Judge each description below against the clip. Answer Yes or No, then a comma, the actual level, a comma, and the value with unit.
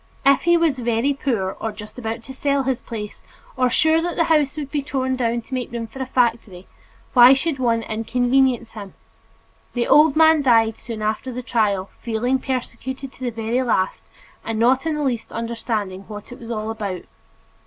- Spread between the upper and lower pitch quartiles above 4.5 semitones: No, average, 3.1 semitones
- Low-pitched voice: No, high, 245 Hz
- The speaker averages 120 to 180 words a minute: No, average, 195 wpm